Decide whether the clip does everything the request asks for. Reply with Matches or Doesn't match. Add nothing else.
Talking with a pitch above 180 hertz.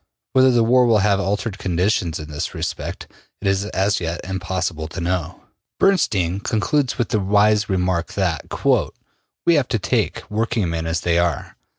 Doesn't match